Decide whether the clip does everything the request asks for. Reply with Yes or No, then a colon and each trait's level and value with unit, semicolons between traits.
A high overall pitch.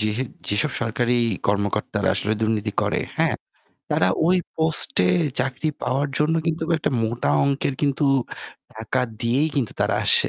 No: low, 120 Hz